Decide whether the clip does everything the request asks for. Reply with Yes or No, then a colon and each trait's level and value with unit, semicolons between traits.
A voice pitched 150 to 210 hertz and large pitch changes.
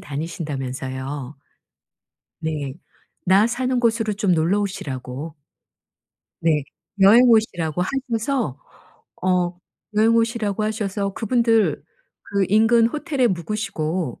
Yes: high, 195 Hz; wide, 6.3 semitones